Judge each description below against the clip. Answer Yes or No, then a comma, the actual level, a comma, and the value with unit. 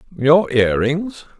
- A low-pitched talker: No, medium, 155 Hz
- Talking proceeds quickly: No, slow, 130 wpm